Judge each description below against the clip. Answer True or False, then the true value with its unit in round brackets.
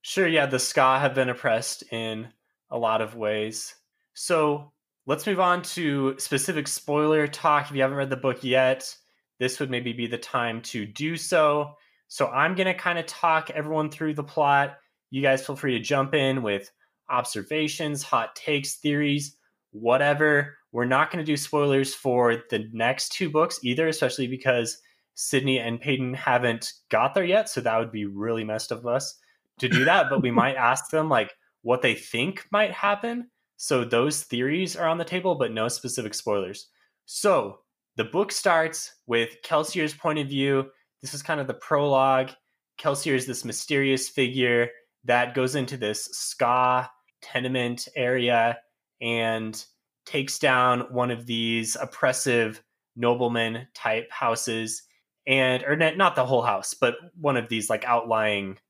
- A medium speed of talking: True (165 wpm)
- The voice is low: True (130 Hz)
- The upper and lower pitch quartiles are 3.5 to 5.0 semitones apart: True (4.0 semitones)